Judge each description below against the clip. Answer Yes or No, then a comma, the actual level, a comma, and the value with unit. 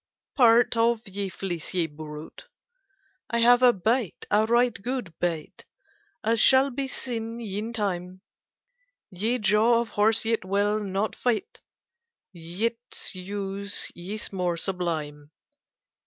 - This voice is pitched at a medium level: No, high, 210 Hz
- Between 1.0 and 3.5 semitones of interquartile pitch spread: No, average, 4.2 semitones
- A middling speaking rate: No, slow, 115 wpm